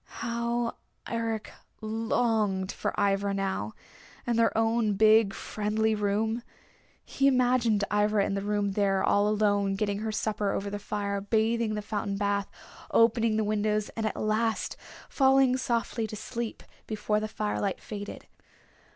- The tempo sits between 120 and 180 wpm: Yes, average, 145 wpm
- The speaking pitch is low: No, high, 215 Hz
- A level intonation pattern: Yes, narrow, 1.9 semitones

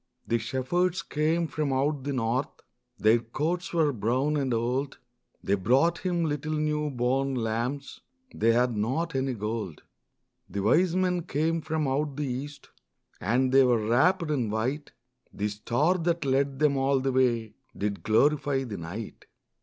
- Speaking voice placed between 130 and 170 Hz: Yes, low, 135 Hz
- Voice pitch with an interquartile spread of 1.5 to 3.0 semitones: No, average, 4.5 semitones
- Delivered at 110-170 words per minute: Yes, average, 155 wpm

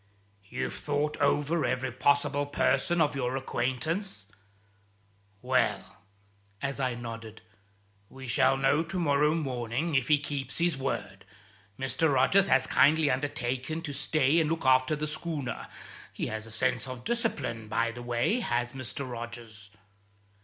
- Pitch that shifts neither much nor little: Yes, average, 3.7 semitones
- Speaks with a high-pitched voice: No, low, 135 Hz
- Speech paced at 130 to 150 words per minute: Yes, average, 140 wpm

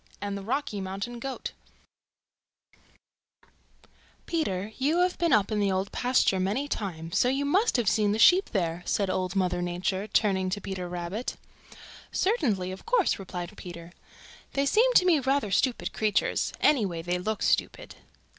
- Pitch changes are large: Yes, wide, 6.5 semitones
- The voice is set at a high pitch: Yes, high, 205 Hz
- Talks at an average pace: Yes, average, 160 wpm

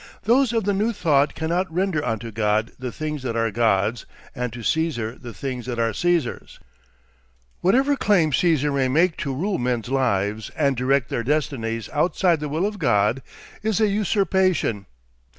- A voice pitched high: No, medium, 140 Hz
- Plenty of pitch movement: Yes, wide, 7.4 semitones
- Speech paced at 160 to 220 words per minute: Yes, average, 170 wpm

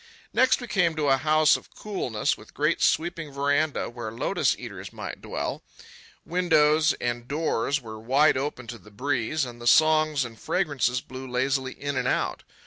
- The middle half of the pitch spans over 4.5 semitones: No, average, 4.1 semitones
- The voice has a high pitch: No, medium, 140 Hz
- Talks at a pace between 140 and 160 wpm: No, average, 170 wpm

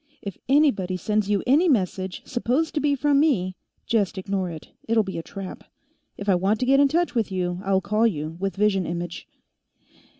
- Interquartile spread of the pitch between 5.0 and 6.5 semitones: Yes, wide, 5.6 semitones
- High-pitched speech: Yes, high, 200 Hz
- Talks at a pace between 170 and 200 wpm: Yes, average, 195 wpm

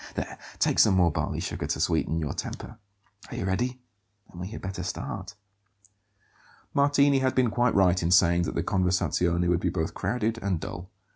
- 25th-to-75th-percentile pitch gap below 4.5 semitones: No, average, 4.9 semitones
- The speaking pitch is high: No, very low, 95 Hz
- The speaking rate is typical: Yes, average, 185 wpm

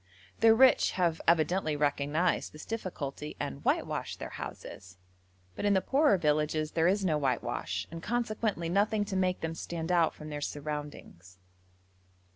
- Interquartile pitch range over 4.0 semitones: Yes, average, 4.5 semitones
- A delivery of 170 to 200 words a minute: No, average, 150 wpm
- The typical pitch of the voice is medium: Yes, medium, 165 Hz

